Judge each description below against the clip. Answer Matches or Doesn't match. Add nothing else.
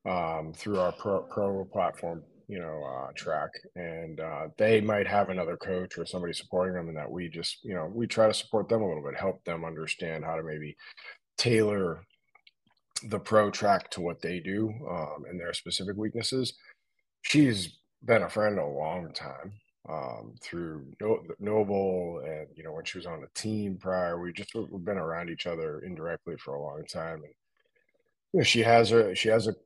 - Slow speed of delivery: Doesn't match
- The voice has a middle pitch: Doesn't match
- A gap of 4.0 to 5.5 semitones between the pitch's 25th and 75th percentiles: Matches